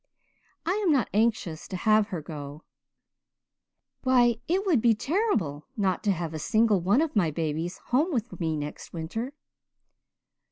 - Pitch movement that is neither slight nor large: No, wide, 7.5 semitones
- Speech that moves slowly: No, average, 155 wpm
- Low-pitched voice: No, high, 210 Hz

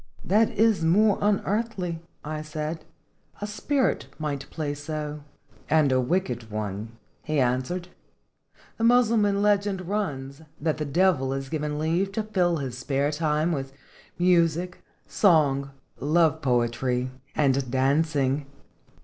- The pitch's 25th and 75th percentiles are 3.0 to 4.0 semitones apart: No, average, 5.3 semitones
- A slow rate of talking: Yes, slow, 125 wpm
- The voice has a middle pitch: Yes, medium, 155 Hz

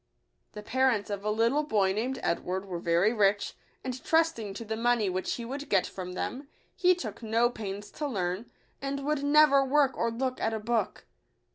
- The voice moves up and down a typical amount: Yes, average, 4.9 semitones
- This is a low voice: No, high, 230 Hz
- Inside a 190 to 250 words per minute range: Yes, average, 195 wpm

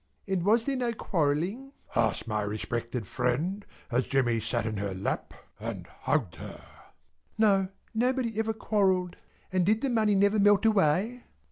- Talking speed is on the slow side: No, average, 150 wpm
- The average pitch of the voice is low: No, high, 190 Hz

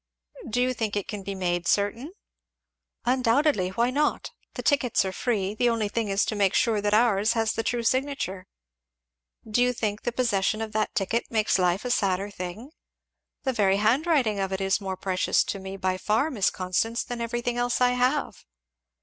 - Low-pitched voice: No, high, 220 Hz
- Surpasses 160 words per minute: Yes, average, 190 wpm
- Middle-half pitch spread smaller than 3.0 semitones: No, average, 3.9 semitones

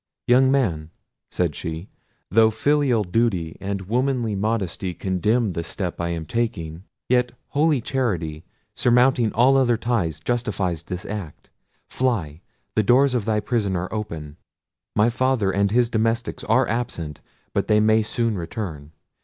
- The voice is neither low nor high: No, low, 110 Hz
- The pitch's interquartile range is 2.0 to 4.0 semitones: No, wide, 5.6 semitones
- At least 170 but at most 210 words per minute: No, average, 145 wpm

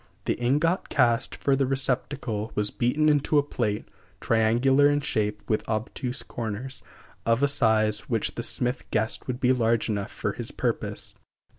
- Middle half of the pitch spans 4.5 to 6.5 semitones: No, average, 3.7 semitones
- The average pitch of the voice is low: Yes, low, 120 Hz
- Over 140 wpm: Yes, average, 160 wpm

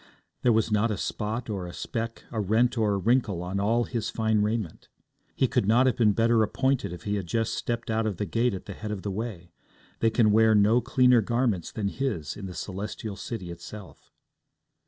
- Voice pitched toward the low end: Yes, low, 110 Hz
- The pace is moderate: No, fast, 215 wpm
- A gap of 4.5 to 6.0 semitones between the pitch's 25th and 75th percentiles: No, average, 2.8 semitones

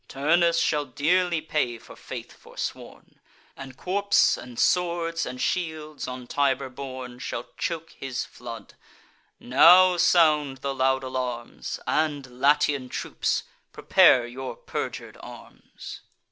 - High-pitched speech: No, medium, 140 Hz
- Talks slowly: Yes, slow, 120 wpm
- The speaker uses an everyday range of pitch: Yes, average, 4.4 semitones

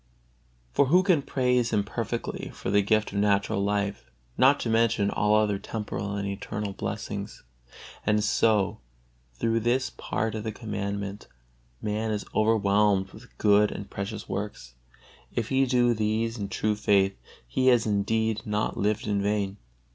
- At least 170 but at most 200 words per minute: No, average, 155 wpm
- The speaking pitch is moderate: No, low, 105 Hz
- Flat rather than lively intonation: Yes, narrow, 2.0 semitones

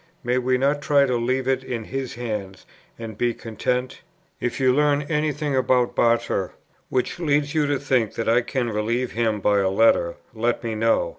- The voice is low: Yes, low, 125 Hz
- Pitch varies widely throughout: No, average, 3.1 semitones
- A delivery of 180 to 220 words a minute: Yes, average, 195 wpm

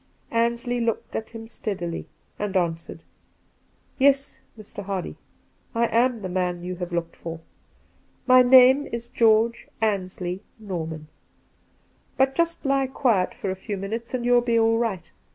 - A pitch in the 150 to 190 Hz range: No, high, 225 Hz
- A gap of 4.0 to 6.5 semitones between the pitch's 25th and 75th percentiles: Yes, average, 4.7 semitones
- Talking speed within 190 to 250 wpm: No, average, 150 wpm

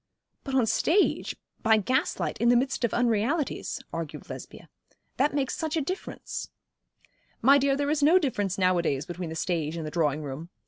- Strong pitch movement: Yes, wide, 8.8 semitones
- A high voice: Yes, high, 235 Hz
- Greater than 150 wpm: Yes, average, 180 wpm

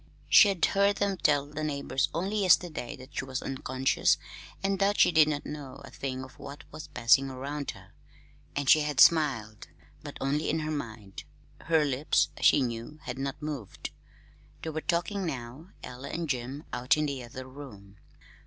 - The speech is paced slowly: No, average, 180 wpm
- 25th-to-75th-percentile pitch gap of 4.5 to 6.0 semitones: No, average, 3.3 semitones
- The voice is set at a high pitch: No, medium, 140 Hz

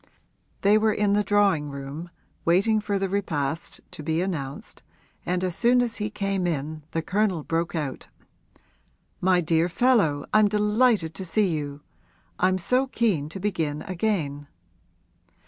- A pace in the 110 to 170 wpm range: Yes, average, 145 wpm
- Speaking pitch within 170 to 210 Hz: Yes, medium, 185 Hz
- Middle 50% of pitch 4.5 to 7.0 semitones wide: Yes, average, 4.8 semitones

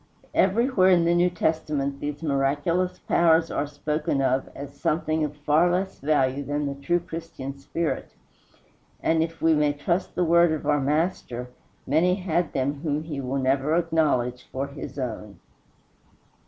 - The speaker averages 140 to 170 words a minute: Yes, average, 155 wpm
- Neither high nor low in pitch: Yes, medium, 150 Hz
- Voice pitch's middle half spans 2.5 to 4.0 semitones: Yes, average, 3.3 semitones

